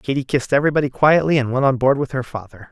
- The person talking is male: Yes, male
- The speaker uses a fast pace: Yes, fast, 245 wpm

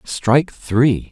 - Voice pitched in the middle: No, low, 125 Hz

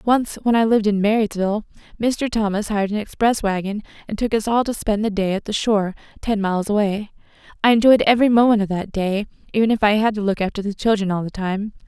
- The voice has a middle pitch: No, high, 210 Hz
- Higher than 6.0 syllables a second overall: Yes, 6.4 syllables/s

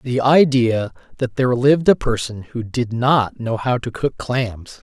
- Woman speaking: No, male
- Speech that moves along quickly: No, average, 185 wpm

